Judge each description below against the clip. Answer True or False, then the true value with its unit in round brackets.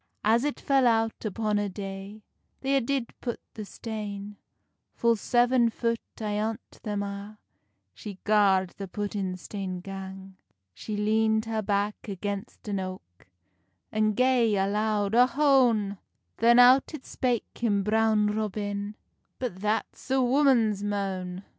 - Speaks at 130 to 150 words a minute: True (135 wpm)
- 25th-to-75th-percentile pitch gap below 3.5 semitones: True (2.6 semitones)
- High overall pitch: True (210 Hz)